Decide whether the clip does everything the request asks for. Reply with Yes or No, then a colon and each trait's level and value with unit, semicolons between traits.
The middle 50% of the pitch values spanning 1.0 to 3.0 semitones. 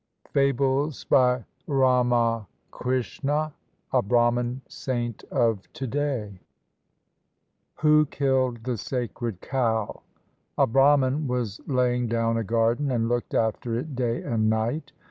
Yes: average, 2.7 semitones